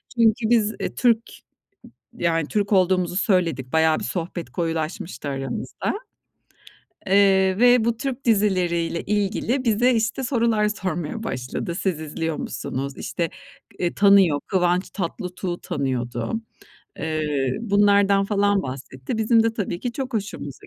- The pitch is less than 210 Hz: Yes, high, 190 Hz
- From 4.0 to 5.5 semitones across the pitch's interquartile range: Yes, average, 5.0 semitones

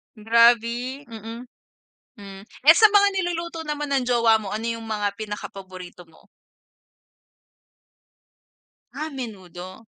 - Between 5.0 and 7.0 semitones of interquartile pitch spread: Yes, average, 5.3 semitones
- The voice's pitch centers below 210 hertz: No, high, 230 Hz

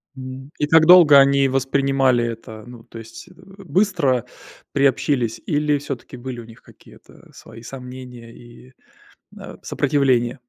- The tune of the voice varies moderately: Yes, average, 3.0 semitones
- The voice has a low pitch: Yes, low, 130 Hz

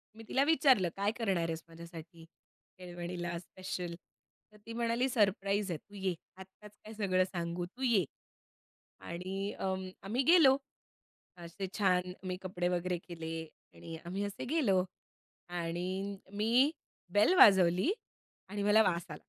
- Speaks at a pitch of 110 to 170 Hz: No, high, 190 Hz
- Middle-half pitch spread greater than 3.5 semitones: No, average, 3.2 semitones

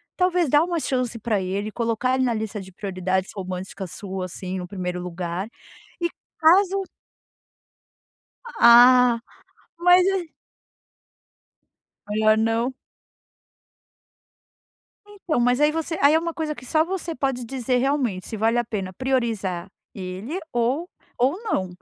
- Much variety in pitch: Yes, wide, 7.8 semitones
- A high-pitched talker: Yes, high, 240 Hz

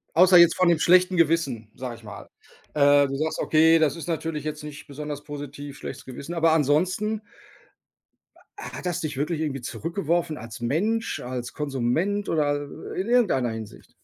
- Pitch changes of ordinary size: Yes, average, 3.5 semitones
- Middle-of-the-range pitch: Yes, medium, 155 Hz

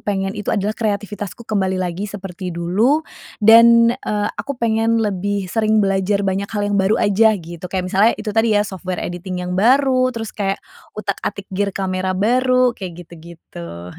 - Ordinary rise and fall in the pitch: Yes, average, 3.1 semitones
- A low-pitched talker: No, high, 200 Hz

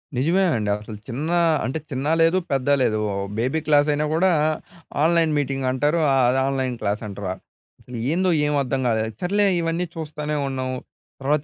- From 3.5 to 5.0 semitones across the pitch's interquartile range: Yes, average, 4.2 semitones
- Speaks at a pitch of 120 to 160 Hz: Yes, medium, 140 Hz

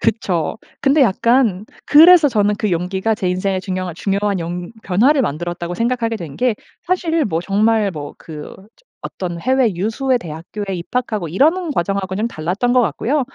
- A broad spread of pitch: Yes, wide, 5.7 semitones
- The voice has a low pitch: No, high, 205 Hz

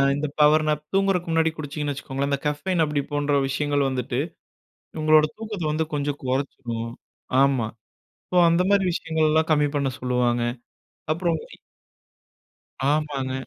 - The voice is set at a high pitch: No, medium, 150 Hz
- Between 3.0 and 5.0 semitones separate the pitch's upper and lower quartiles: No, narrow, 2.6 semitones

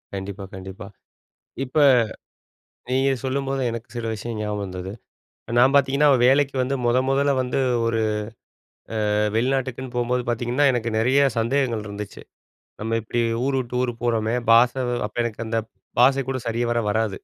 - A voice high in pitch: No, low, 120 Hz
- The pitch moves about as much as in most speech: Yes, average, 3.1 semitones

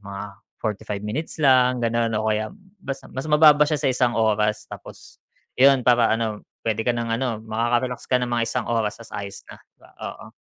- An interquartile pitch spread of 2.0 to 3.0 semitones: Yes, narrow, 2.6 semitones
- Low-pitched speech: Yes, low, 115 Hz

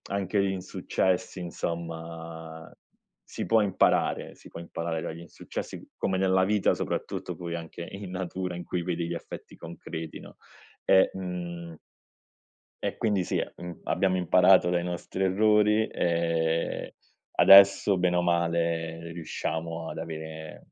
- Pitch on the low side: Yes, very low, 85 Hz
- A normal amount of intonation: No, narrow, 2.2 semitones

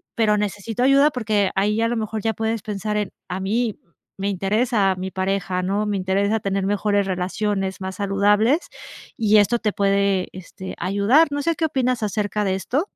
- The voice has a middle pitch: No, high, 205 Hz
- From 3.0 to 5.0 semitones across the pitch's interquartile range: No, narrow, 2.5 semitones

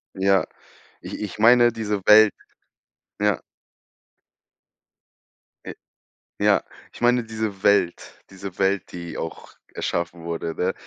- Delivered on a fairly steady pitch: No, average, 3.4 semitones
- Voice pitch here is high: No, low, 100 Hz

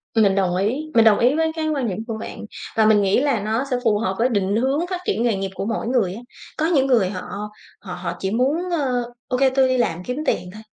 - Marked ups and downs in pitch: No, average, 4.7 semitones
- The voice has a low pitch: No, high, 230 Hz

